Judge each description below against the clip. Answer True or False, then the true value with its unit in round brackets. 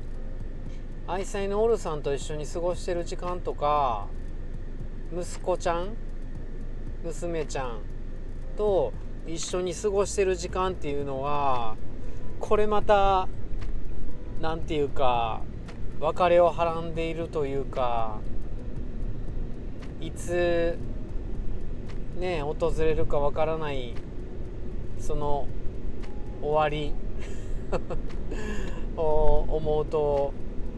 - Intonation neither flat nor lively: False (5.9 semitones)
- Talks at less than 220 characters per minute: True (175 characters per minute)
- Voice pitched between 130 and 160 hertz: True (140 Hz)